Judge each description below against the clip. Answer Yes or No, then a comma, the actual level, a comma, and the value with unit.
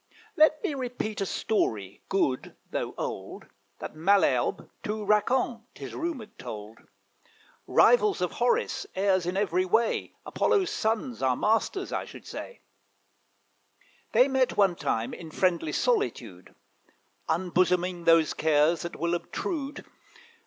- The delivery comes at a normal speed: No, slow, 125 wpm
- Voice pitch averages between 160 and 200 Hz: Yes, high, 190 Hz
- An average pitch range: No, wide, 7.5 semitones